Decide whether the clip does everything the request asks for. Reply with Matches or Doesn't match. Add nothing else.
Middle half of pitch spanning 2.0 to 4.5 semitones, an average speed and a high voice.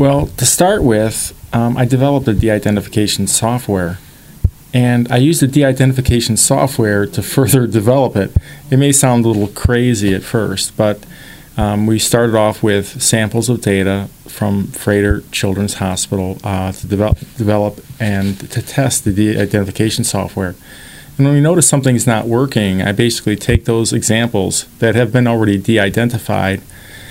Doesn't match